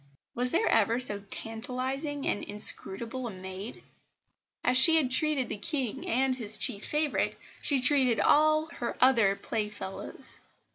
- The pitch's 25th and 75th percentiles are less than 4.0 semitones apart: No, average, 4.3 semitones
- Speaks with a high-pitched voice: Yes, very high, 250 Hz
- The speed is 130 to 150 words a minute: Yes, average, 145 wpm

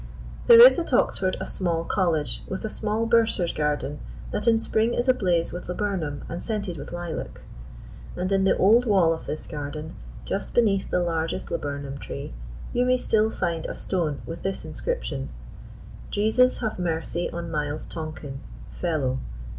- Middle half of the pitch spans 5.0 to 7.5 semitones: Yes, wide, 5.5 semitones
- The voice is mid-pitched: Yes, medium, 180 Hz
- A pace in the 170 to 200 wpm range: No, average, 160 wpm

